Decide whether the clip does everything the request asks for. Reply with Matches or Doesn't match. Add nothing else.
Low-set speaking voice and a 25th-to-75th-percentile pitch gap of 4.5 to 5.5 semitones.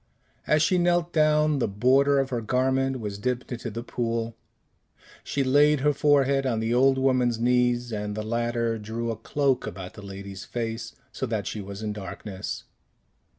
Doesn't match